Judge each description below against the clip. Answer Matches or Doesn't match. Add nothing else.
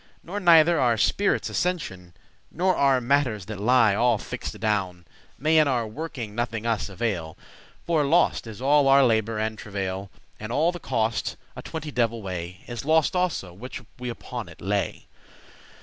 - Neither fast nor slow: Matches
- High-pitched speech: Doesn't match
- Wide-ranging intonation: Matches